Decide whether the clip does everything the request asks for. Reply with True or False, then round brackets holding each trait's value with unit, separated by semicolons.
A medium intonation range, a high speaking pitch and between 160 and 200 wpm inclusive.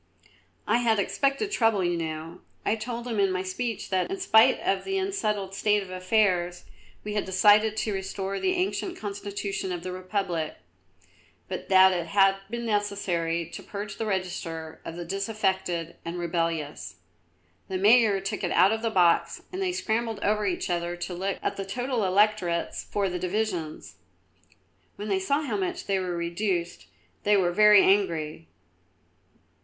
True (3.5 semitones; 195 Hz; 165 wpm)